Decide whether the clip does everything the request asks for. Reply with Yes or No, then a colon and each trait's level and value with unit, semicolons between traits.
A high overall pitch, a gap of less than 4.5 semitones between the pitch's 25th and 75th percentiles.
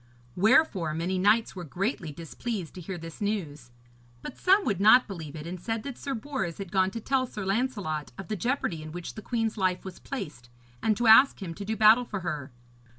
No: high, 195 Hz; average, 5.0 semitones